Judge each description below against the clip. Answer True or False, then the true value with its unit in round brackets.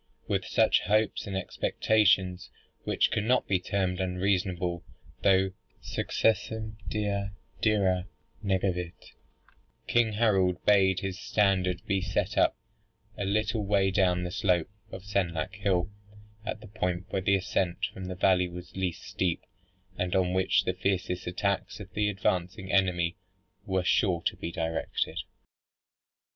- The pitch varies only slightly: True (1.8 semitones)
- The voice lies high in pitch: False (95 Hz)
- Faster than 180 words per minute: False (135 wpm)